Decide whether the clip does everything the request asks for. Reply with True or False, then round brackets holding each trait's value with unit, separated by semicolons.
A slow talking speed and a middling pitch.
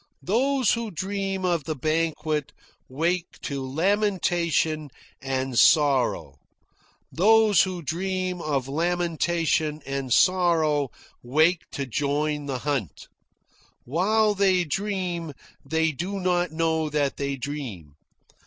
True (105 wpm; 160 Hz)